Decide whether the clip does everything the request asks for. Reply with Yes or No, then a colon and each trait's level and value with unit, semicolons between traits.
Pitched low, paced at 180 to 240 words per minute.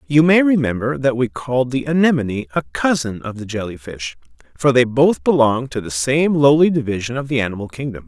Yes: low, 130 Hz; average, 200 wpm